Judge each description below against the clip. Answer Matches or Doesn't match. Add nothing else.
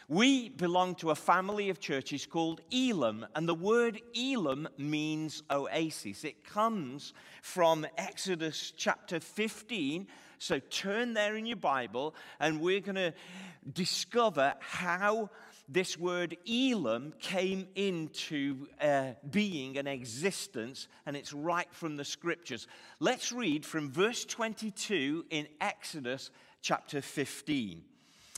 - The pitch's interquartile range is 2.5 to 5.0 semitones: Doesn't match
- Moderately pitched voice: Matches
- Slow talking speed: Matches